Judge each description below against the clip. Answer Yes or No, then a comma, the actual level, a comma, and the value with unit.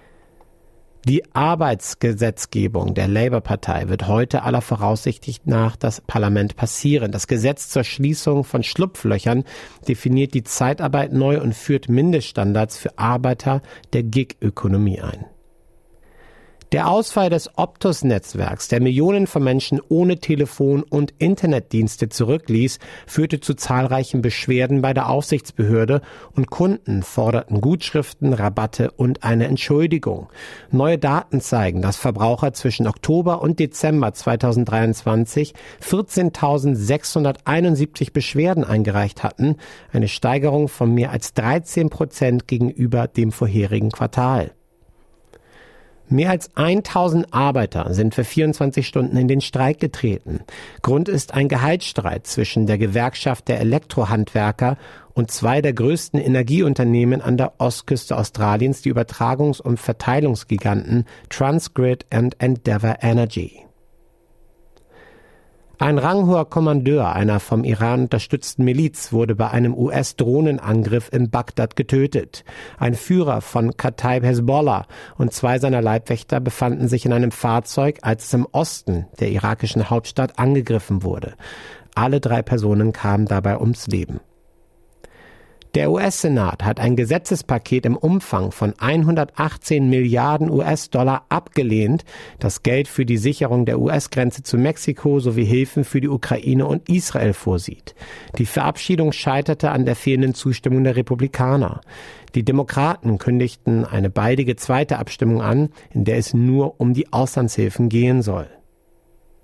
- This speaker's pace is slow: Yes, slow, 120 wpm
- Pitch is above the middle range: No, low, 125 Hz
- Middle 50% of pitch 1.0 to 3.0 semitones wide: No, average, 4.0 semitones